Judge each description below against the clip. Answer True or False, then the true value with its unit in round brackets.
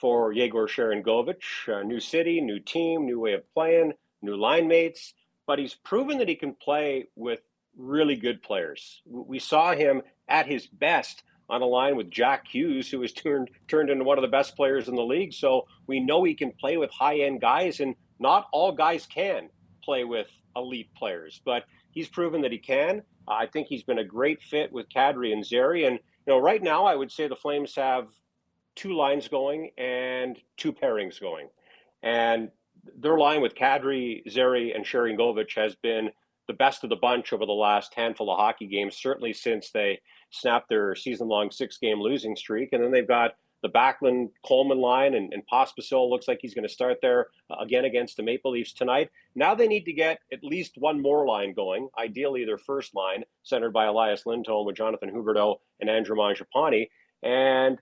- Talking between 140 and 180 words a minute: False (195 wpm)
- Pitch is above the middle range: False (130 Hz)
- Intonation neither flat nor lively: False (5.7 semitones)